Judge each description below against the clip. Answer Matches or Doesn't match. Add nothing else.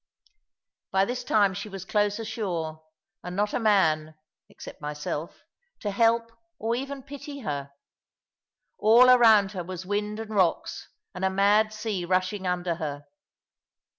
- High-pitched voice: Matches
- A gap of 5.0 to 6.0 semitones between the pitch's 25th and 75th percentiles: Doesn't match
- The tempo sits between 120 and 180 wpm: Matches